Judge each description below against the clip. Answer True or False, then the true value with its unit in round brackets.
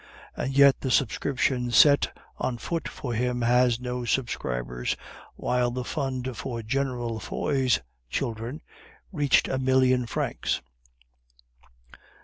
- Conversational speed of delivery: False (115 wpm)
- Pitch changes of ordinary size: False (2.0 semitones)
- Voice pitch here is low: True (125 Hz)